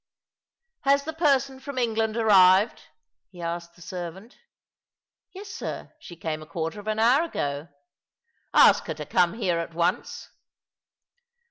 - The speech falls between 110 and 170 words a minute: Yes, average, 150 wpm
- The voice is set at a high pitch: Yes, high, 205 Hz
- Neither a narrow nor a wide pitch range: No, wide, 7.5 semitones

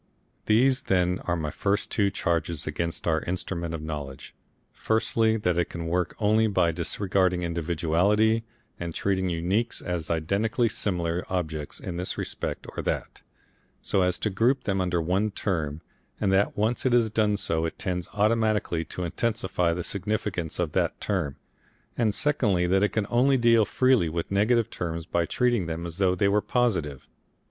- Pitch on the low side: Yes, very low, 95 Hz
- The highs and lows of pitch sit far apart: No, average, 4.2 semitones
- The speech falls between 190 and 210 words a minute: No, average, 170 wpm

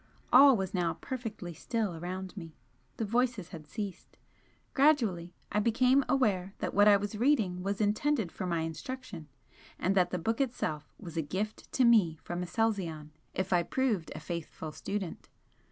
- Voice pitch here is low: No, high, 195 Hz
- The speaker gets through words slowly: No, average, 165 wpm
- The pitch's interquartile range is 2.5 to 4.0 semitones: No, average, 4.8 semitones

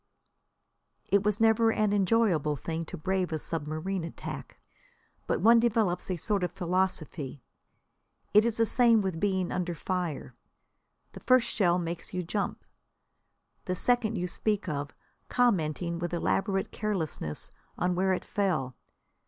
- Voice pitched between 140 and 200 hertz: Yes, medium, 185 Hz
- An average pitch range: Yes, average, 3.9 semitones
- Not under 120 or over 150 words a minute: Yes, slow, 135 wpm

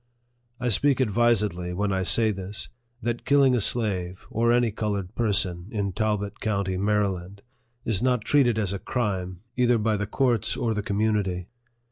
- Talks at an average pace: Yes, average, 165 wpm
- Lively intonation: No, average, 3.5 semitones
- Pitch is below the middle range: Yes, low, 105 Hz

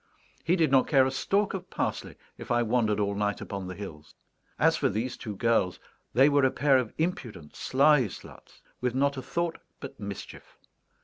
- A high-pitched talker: No, low, 130 Hz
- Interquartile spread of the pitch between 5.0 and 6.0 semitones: Yes, wide, 5.4 semitones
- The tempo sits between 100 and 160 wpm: No, average, 190 wpm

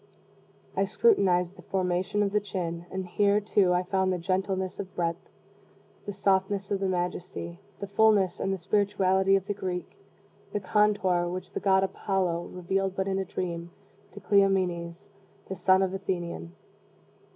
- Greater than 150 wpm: Yes, average, 165 wpm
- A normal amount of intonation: No, narrow, 1.6 semitones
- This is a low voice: No, high, 190 Hz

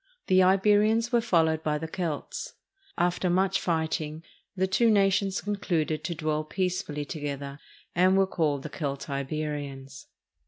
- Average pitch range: Yes, average, 4.1 semitones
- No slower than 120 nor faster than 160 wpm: Yes, slow, 135 wpm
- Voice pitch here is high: No, medium, 165 Hz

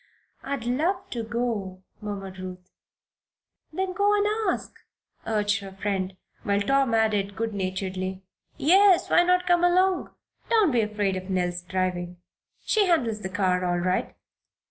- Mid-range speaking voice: No, high, 210 Hz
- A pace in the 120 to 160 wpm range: Yes, average, 145 wpm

